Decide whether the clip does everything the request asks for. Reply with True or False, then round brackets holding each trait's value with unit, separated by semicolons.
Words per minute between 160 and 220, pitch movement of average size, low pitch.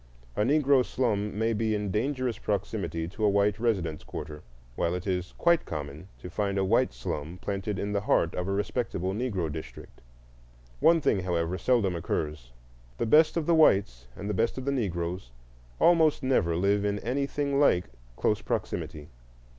False (170 wpm; 5.8 semitones; 100 Hz)